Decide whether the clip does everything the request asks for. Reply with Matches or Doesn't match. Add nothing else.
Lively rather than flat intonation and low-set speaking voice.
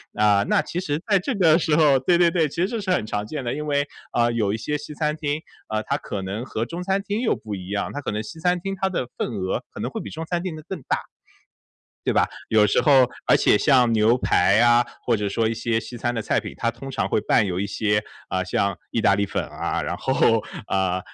Matches